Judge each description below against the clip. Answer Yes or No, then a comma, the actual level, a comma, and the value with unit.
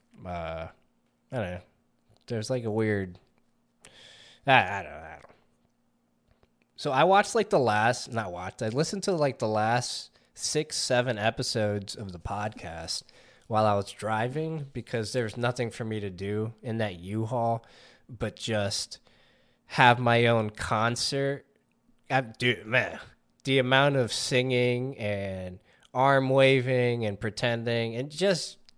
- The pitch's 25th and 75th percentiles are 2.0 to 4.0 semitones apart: Yes, average, 3.4 semitones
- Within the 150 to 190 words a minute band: No, average, 140 wpm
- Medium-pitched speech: No, low, 115 Hz